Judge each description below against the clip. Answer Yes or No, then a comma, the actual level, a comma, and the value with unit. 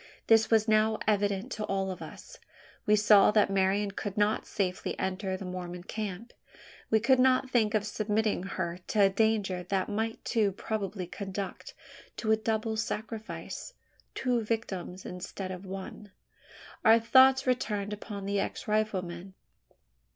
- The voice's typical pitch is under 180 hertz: No, high, 210 Hz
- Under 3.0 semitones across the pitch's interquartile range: Yes, narrow, 2.4 semitones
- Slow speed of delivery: No, average, 150 wpm